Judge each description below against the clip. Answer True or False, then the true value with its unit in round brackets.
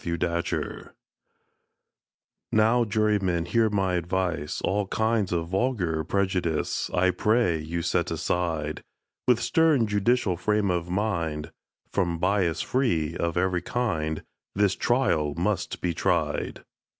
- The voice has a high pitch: False (90 Hz)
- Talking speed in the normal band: False (125 wpm)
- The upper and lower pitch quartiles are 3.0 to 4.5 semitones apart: True (4.2 semitones)